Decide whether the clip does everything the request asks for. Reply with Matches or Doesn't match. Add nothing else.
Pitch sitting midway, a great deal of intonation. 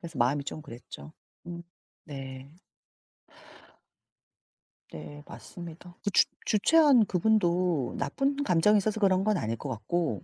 Matches